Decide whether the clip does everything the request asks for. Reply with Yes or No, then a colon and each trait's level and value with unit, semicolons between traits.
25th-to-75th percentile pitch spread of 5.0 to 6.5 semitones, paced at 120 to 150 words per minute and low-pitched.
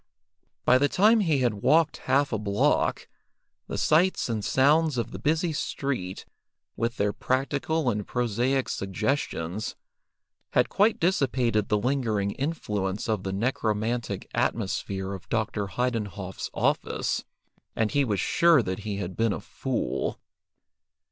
Yes: wide, 5.6 semitones; slow, 135 wpm; low, 115 Hz